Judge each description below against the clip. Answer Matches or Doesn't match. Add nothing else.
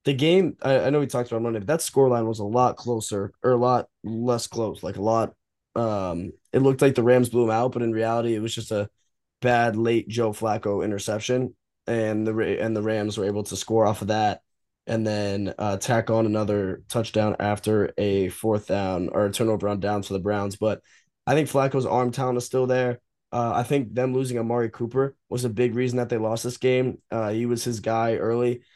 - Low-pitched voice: Matches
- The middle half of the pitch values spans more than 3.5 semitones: Doesn't match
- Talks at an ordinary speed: Doesn't match